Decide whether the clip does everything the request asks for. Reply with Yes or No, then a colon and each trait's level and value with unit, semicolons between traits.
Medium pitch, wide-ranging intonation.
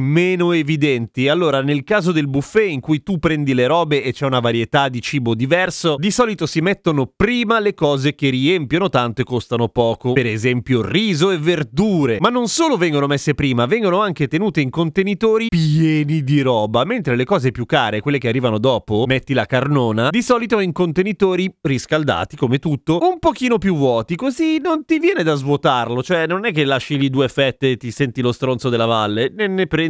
Yes: medium, 150 Hz; wide, 6.2 semitones